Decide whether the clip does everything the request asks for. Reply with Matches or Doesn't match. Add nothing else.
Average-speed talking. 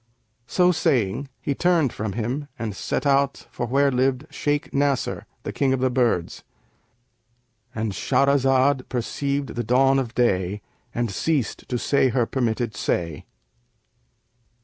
Doesn't match